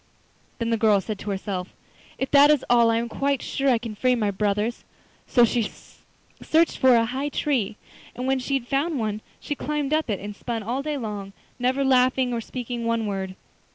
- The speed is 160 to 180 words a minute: No, fast, 205 wpm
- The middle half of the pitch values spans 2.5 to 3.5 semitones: No, average, 3.9 semitones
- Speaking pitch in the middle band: No, high, 240 Hz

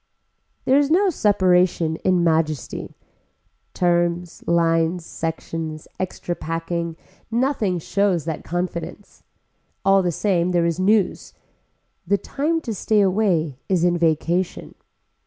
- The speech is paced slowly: Yes, slow, 115 wpm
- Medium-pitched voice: Yes, medium, 175 Hz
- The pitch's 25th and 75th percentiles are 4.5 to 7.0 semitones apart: No, average, 3.2 semitones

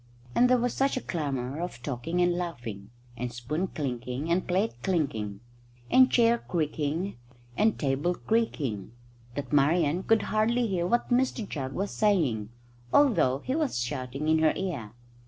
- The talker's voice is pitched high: No, medium, 160 Hz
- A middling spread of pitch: No, wide, 8.5 semitones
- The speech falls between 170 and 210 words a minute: No, average, 155 wpm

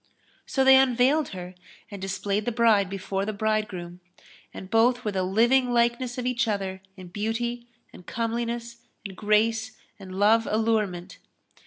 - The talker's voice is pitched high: Yes, high, 220 Hz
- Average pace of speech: Yes, average, 150 wpm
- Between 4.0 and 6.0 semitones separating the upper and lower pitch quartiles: No, average, 3.4 semitones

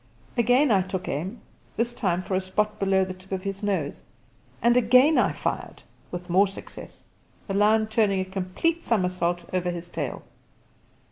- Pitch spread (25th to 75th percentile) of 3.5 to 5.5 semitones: No, average, 3.1 semitones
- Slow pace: No, average, 165 wpm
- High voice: Yes, high, 195 Hz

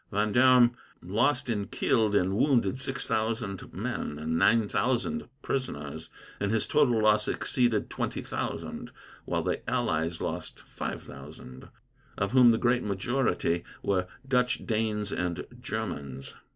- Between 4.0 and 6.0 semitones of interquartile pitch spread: Yes, average, 4.6 semitones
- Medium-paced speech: No, slow, 130 wpm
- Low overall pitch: Yes, low, 110 Hz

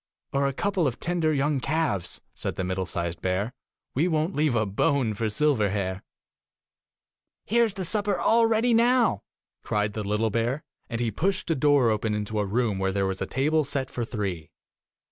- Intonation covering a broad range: Yes, wide, 7.4 semitones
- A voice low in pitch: Yes, low, 125 Hz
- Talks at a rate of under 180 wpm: No, average, 190 wpm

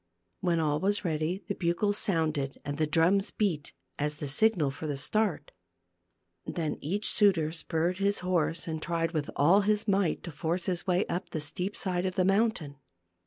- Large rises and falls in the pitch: No, average, 3.9 semitones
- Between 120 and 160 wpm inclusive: No, average, 180 wpm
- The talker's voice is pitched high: No, medium, 170 Hz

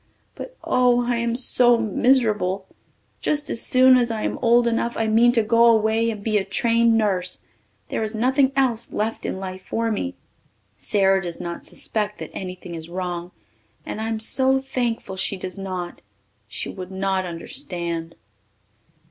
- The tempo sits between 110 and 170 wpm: Yes, average, 165 wpm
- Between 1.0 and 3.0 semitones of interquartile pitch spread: No, average, 4.0 semitones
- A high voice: Yes, high, 220 Hz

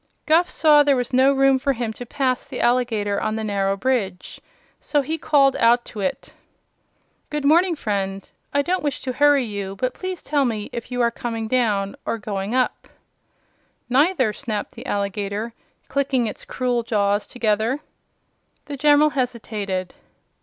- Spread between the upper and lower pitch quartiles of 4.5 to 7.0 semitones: Yes, average, 4.8 semitones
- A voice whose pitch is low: No, high, 245 Hz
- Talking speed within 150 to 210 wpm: Yes, average, 160 wpm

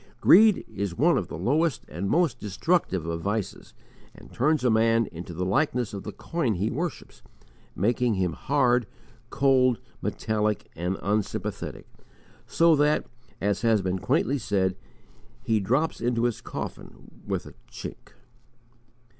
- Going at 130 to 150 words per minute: Yes, average, 140 wpm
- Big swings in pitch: Yes, wide, 5.7 semitones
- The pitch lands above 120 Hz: No, low, 115 Hz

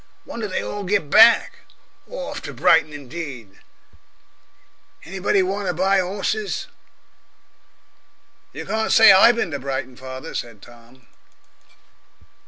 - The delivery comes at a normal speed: No, slow, 115 wpm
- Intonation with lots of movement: Yes, wide, 7.5 semitones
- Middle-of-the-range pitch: Yes, medium, 180 Hz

